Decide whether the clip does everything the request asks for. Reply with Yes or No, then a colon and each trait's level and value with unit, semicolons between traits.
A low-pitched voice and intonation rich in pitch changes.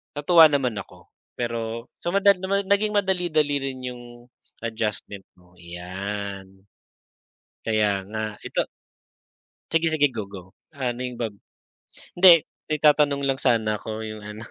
Yes: low, 120 Hz; wide, 6.4 semitones